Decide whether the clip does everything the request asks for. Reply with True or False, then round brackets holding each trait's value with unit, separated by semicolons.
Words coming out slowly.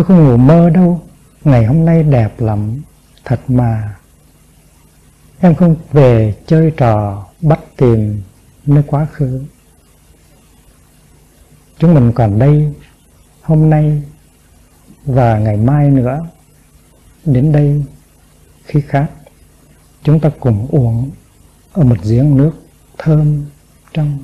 True (115 wpm)